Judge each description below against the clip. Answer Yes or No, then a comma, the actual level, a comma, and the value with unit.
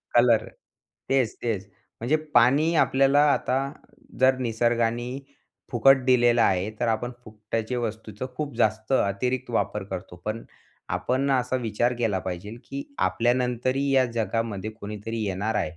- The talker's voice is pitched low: Yes, low, 120 Hz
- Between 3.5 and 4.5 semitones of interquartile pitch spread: No, average, 2.9 semitones